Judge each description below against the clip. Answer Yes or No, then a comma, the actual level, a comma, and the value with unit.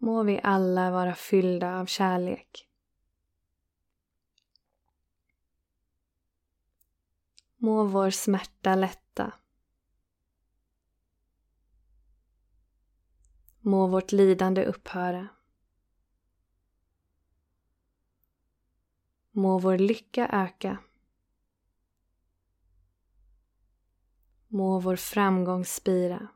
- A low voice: Yes, very low, 90 Hz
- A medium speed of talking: No, slow, 50 wpm